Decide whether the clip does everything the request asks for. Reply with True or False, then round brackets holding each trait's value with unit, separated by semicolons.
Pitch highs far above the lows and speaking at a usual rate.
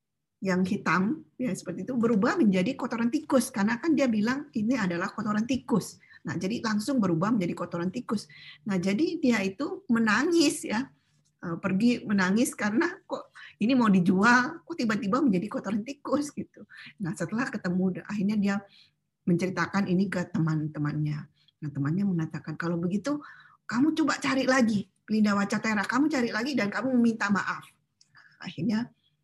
False (5.8 semitones; 145 wpm)